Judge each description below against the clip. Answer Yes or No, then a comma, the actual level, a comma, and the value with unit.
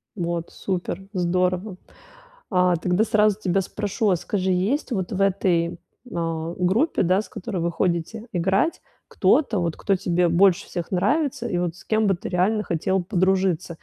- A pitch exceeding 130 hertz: Yes, medium, 185 Hz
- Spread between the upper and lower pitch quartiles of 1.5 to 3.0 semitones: Yes, average, 2.7 semitones